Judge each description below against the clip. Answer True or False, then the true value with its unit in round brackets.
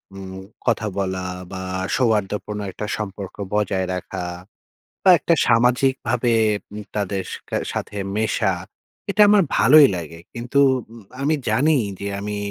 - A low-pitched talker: True (105 Hz)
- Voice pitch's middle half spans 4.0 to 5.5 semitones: True (4.4 semitones)